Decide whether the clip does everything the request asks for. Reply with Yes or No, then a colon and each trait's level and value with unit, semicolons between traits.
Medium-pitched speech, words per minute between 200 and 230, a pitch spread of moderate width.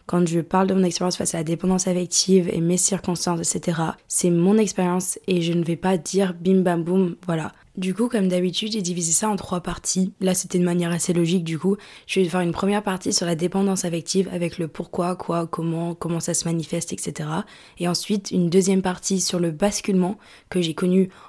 No: medium, 180 Hz; average, 215 wpm; narrow, 1.7 semitones